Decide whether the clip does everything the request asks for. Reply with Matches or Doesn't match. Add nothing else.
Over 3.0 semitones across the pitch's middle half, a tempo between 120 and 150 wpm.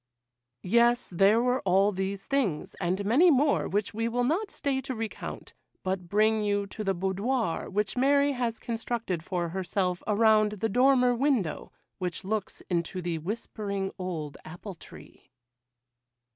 Matches